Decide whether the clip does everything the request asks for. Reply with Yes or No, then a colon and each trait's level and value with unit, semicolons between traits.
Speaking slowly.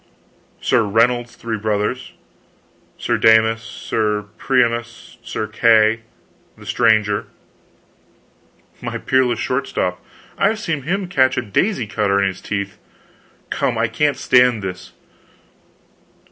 Yes: slow, 120 wpm